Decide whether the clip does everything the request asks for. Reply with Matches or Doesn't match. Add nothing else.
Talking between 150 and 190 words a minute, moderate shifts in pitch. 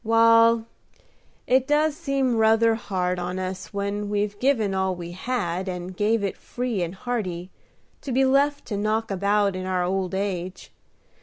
Matches